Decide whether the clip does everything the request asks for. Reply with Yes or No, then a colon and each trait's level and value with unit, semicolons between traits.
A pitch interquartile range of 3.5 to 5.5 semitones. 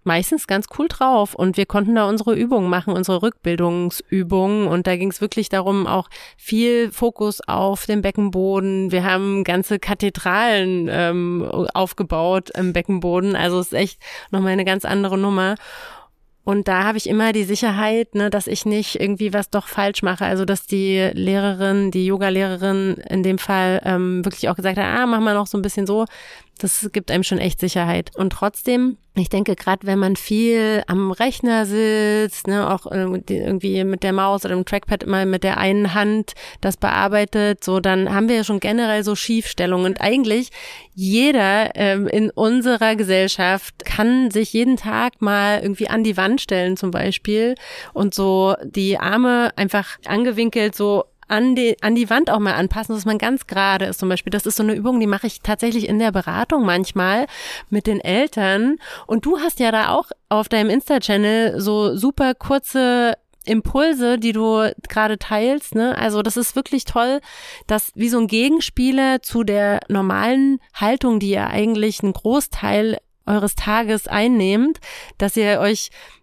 No: average, 2.9 semitones